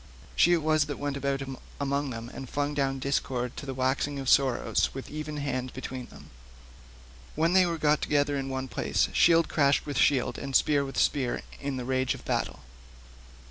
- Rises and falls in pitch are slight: Yes, narrow, 1.9 semitones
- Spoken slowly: No, average, 190 wpm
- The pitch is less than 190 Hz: Yes, medium, 140 Hz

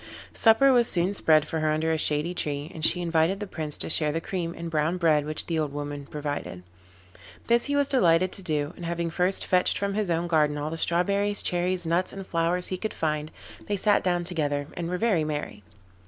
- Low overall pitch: No, medium, 170 Hz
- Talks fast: Yes, fast, 220 wpm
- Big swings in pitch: No, average, 3.2 semitones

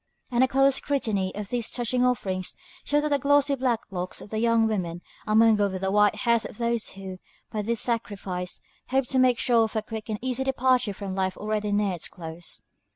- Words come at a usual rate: No, fast, 220 wpm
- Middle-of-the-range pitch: No, high, 220 Hz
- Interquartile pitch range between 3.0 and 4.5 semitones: Yes, average, 4.2 semitones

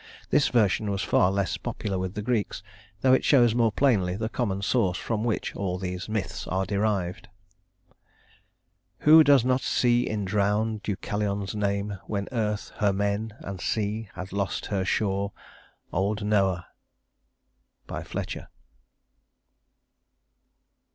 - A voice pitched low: Yes, low, 105 Hz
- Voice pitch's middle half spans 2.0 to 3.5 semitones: Yes, narrow, 2.4 semitones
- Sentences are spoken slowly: Yes, slow, 130 wpm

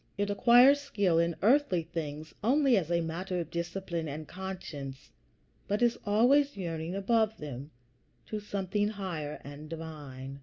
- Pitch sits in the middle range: Yes, medium, 180 Hz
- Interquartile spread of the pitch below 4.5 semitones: No, average, 4.9 semitones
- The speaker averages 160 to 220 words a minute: No, average, 145 wpm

